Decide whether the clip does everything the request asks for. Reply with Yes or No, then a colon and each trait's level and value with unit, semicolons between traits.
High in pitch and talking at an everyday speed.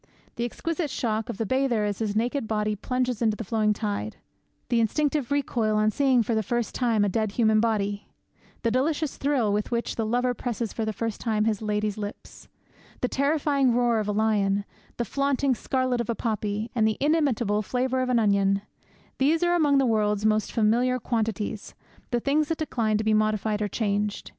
Yes: high, 225 Hz; average, 195 wpm